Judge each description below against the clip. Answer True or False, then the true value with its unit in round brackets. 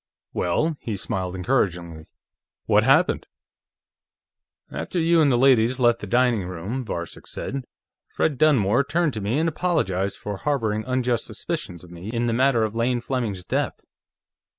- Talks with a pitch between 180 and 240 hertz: False (120 Hz)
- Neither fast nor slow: True (150 wpm)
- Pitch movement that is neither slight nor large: False (5.7 semitones)